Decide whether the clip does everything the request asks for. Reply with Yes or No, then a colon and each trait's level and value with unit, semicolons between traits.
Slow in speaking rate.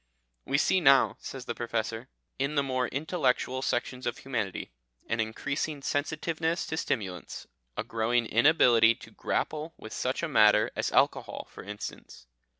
No: average, 150 wpm